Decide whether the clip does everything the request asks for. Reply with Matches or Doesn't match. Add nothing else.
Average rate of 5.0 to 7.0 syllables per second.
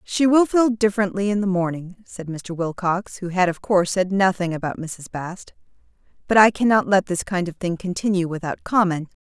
Matches